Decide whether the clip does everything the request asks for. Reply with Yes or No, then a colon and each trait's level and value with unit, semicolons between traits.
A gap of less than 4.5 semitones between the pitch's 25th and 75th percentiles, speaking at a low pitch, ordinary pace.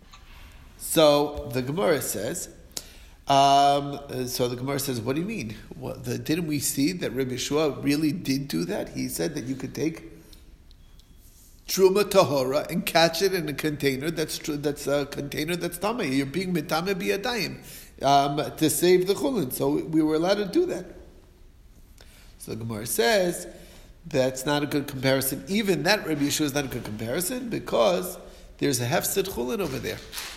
No: average, 4.0 semitones; medium, 145 Hz; average, 170 wpm